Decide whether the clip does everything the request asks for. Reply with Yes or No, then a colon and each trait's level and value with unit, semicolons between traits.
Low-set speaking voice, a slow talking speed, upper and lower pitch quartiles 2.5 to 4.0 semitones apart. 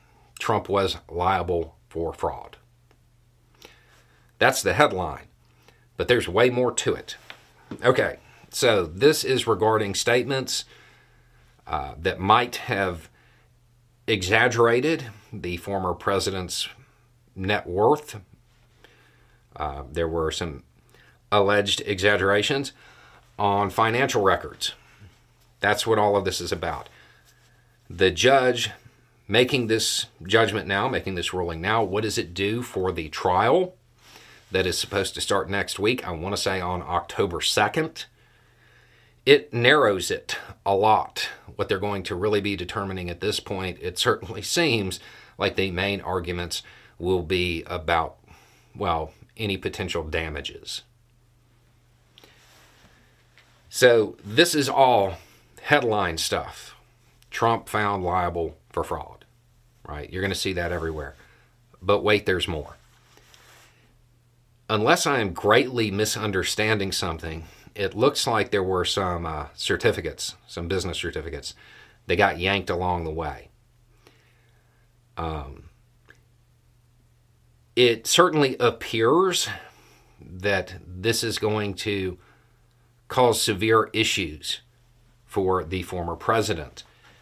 No: low, 110 Hz; slow, 115 wpm; average, 4.4 semitones